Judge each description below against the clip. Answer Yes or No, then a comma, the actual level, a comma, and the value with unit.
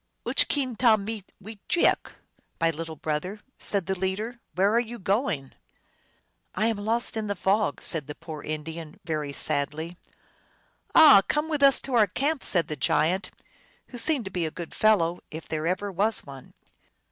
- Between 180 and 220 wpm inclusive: Yes, average, 190 wpm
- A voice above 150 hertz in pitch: Yes, high, 190 Hz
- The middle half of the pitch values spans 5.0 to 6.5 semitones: Yes, wide, 5.6 semitones